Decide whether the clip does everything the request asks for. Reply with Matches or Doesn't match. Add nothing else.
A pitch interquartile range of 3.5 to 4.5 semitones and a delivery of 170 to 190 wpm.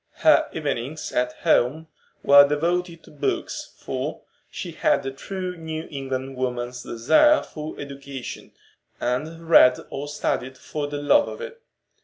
Doesn't match